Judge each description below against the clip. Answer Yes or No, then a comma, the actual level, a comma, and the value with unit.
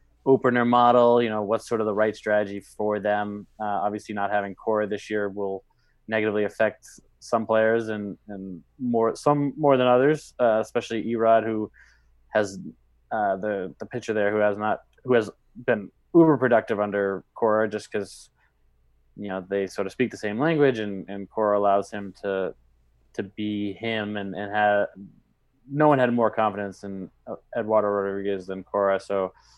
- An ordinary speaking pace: Yes, average, 175 wpm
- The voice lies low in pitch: Yes, low, 105 Hz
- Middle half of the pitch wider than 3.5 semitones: No, narrow, 2.4 semitones